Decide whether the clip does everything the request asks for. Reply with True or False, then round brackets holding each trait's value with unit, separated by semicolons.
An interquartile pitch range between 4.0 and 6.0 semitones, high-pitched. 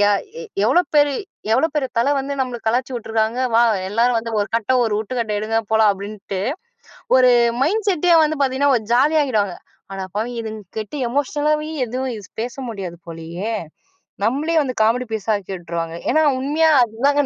True (4.7 semitones; 240 Hz)